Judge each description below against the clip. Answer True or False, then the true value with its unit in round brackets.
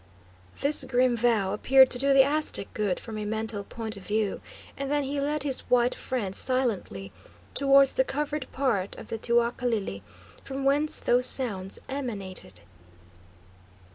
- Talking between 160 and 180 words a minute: False (150 wpm)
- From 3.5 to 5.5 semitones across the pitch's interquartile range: True (4.5 semitones)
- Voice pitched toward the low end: False (245 Hz)